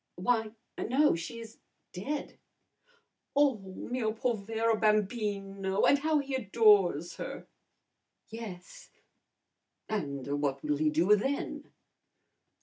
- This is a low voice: No, high, 215 Hz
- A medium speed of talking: No, slow, 100 wpm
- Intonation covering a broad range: No, average, 4.5 semitones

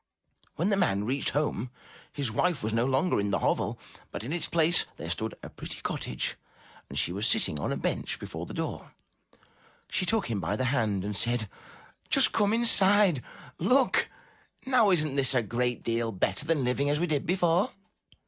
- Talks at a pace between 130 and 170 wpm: No, average, 185 wpm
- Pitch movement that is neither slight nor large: No, wide, 7.9 semitones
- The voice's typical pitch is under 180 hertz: Yes, low, 135 Hz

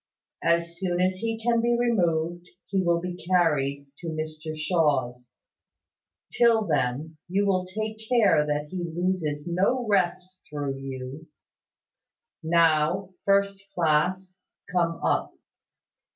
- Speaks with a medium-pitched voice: Yes, medium, 175 Hz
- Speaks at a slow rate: Yes, slow, 120 wpm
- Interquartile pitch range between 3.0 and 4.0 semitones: Yes, average, 3.5 semitones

